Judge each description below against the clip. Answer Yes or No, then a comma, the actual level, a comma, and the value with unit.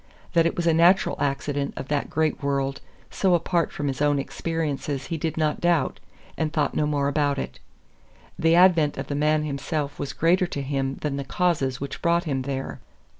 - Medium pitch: Yes, medium, 150 Hz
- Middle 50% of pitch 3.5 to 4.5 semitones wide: No, average, 2.9 semitones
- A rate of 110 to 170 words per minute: No, average, 195 wpm